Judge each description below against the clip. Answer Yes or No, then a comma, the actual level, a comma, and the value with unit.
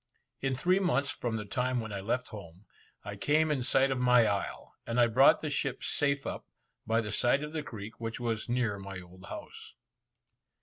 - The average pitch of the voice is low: Yes, low, 120 Hz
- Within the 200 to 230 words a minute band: Yes, fast, 205 wpm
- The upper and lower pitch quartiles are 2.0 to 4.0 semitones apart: No, average, 4.5 semitones